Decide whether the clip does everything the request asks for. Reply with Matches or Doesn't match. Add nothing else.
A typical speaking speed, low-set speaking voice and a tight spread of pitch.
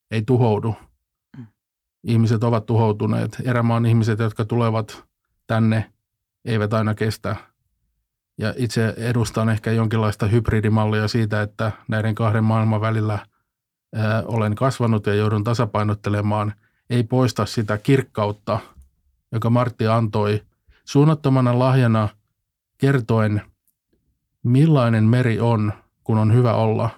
Matches